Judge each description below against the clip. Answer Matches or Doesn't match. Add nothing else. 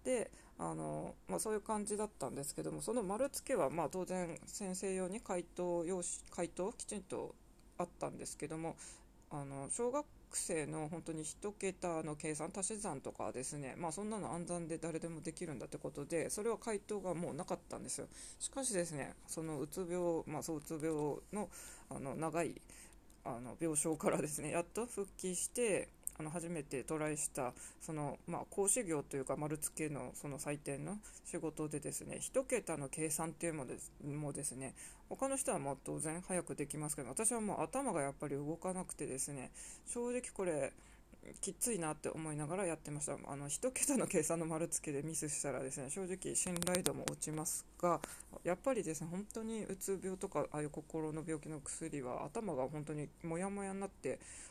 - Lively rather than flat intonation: Doesn't match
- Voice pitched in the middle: Matches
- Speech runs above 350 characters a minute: Matches